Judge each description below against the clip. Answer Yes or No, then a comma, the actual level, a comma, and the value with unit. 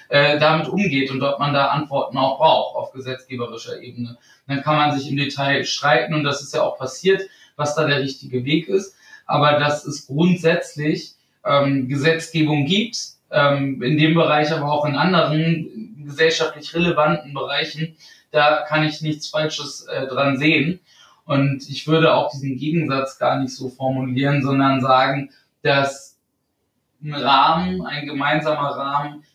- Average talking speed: Yes, average, 145 wpm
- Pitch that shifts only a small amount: Yes, narrow, 2.3 semitones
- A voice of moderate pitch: Yes, medium, 145 Hz